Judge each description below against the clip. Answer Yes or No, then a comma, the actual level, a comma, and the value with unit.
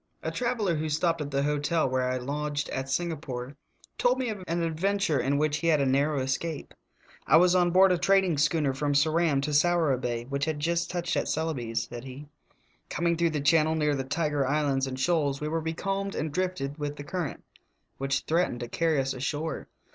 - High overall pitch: No, medium, 150 Hz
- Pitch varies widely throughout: No, average, 3.5 semitones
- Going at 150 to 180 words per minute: No, average, 200 wpm